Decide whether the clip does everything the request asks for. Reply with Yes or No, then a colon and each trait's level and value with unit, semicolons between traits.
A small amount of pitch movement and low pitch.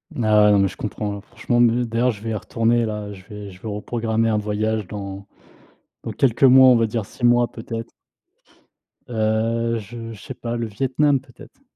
Yes: narrow, 2.3 semitones; low, 115 Hz